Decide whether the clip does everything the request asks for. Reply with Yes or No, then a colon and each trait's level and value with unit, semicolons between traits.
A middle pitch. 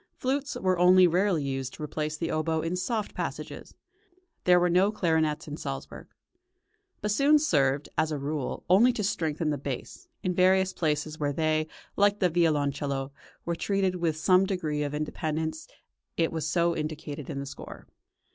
Yes: medium, 160 Hz